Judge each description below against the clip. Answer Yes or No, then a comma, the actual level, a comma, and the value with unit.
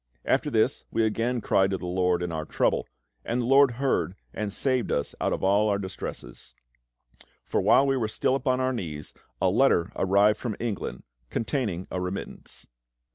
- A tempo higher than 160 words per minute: Yes, average, 180 wpm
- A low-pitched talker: Yes, low, 105 Hz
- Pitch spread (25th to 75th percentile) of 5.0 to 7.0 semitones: Yes, wide, 5.4 semitones